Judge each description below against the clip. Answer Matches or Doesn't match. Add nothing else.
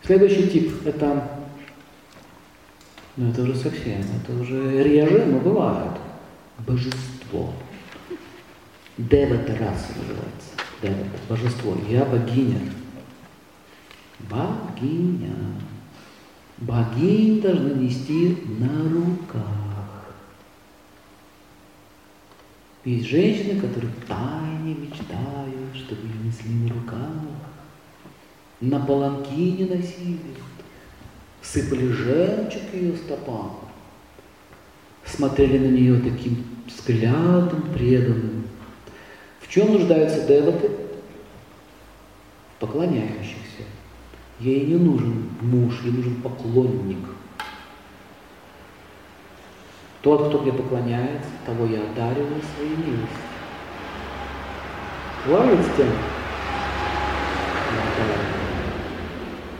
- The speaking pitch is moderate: Doesn't match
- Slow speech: Matches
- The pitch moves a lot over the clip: Matches